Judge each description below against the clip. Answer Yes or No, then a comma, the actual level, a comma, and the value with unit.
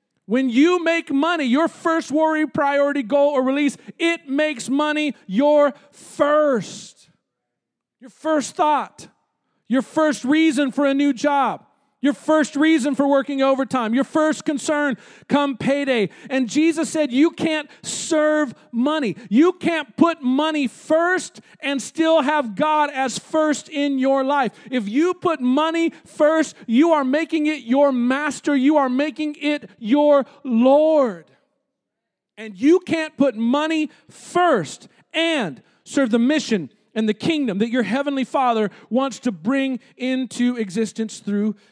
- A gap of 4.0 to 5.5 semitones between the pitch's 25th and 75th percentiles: No, average, 3.4 semitones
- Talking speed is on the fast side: No, average, 140 wpm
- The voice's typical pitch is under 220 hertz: No, very high, 285 Hz